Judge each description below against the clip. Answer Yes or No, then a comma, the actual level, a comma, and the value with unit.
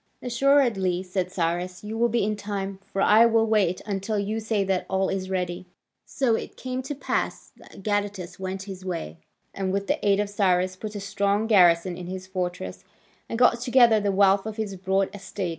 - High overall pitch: Yes, high, 195 Hz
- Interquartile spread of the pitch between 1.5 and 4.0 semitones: Yes, narrow, 2.6 semitones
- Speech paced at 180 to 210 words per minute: Yes, average, 195 wpm